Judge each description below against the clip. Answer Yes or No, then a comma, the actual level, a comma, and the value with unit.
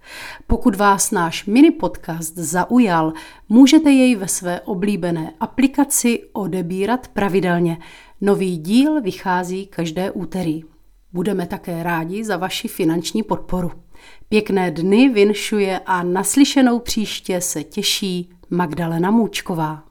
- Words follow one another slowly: Yes, slow, 110 wpm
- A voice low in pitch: No, high, 190 Hz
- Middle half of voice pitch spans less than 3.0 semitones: No, average, 3.7 semitones